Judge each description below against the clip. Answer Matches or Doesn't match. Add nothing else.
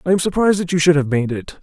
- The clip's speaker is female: Doesn't match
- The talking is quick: Matches